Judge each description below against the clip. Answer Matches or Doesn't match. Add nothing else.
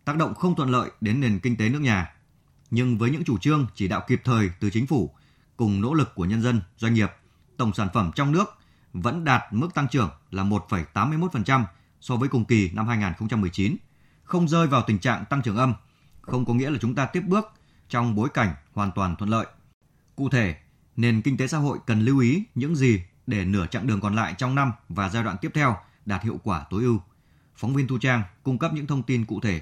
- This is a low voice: Matches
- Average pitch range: Matches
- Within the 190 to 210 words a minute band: Doesn't match